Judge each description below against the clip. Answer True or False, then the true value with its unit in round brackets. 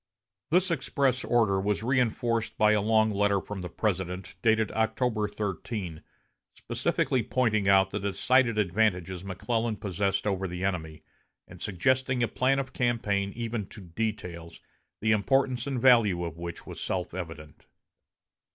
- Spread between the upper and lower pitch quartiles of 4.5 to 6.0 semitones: False (3.8 semitones)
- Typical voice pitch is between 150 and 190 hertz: False (105 Hz)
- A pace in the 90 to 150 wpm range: True (140 wpm)